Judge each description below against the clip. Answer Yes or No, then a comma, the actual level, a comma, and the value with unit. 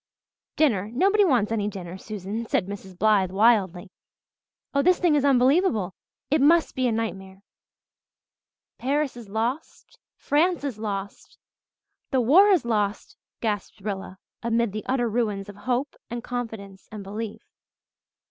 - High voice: Yes, high, 225 Hz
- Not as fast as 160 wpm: Yes, average, 140 wpm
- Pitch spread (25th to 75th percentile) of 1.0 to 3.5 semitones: No, average, 4.9 semitones